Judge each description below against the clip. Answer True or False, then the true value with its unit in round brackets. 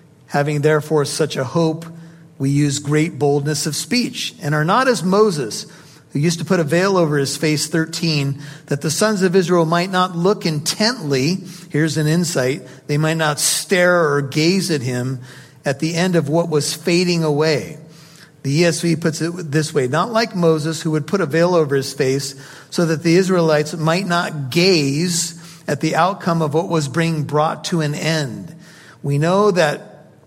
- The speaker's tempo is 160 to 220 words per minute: True (180 wpm)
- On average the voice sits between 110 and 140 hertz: False (160 Hz)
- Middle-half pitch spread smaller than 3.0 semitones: True (2.5 semitones)